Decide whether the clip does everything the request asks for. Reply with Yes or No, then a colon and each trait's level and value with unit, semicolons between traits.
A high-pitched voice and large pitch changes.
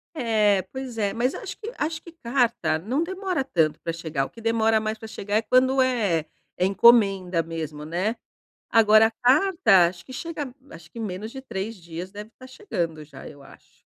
Yes: high, 220 Hz; wide, 6.8 semitones